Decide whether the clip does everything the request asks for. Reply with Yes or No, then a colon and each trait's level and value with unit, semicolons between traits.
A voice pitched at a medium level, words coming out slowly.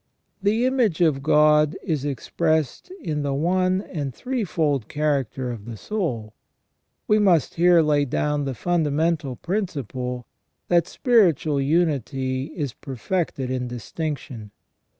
Yes: medium, 150 Hz; slow, 120 wpm